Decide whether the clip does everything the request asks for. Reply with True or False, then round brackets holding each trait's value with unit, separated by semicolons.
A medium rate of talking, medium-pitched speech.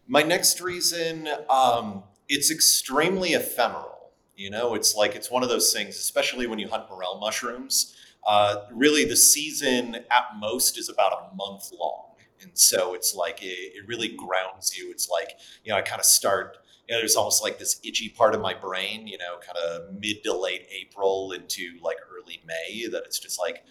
True (190 wpm; 150 Hz)